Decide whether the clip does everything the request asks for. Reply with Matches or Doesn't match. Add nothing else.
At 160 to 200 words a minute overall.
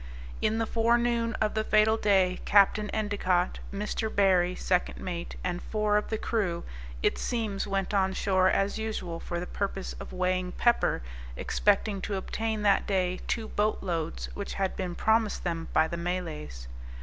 Matches